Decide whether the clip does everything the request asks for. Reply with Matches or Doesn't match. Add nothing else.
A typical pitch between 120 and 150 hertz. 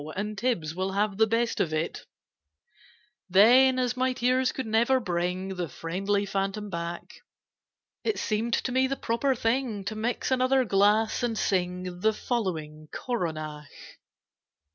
Doesn't match